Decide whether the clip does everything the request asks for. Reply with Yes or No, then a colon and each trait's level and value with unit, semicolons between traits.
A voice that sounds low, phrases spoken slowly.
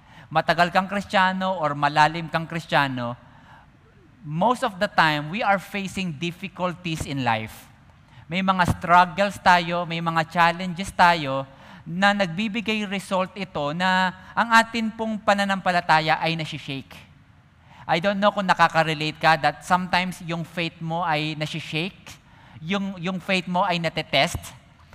No: medium, 175 Hz; slow, 130 wpm